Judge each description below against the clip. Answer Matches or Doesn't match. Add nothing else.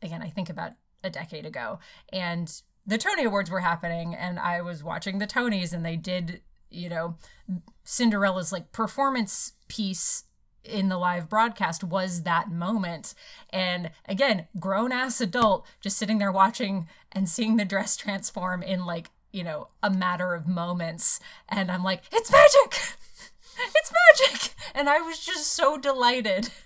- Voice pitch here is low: Doesn't match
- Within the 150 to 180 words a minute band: Matches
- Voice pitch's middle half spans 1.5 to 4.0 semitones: Doesn't match